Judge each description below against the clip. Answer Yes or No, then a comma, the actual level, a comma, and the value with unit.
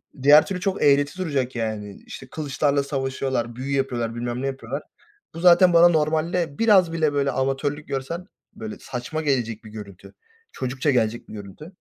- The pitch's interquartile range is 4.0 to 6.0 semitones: Yes, average, 4.4 semitones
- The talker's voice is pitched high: No, medium, 140 Hz